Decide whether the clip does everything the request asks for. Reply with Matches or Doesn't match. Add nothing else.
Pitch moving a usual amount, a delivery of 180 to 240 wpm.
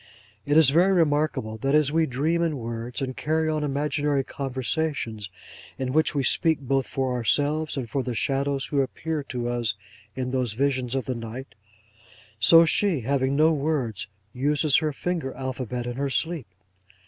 Doesn't match